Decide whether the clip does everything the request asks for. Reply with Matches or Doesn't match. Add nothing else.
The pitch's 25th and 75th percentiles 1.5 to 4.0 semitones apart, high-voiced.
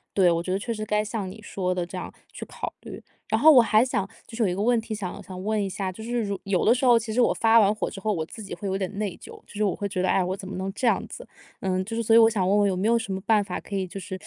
Matches